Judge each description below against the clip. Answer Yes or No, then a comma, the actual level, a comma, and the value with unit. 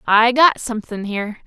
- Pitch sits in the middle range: No, high, 225 Hz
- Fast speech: No, average, 165 wpm